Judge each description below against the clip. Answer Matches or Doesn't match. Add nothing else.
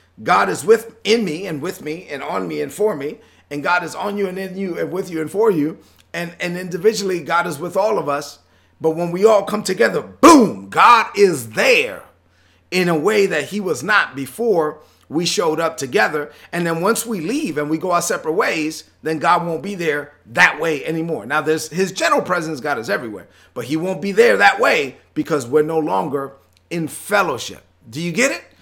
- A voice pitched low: Doesn't match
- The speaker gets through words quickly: Matches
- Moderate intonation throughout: Matches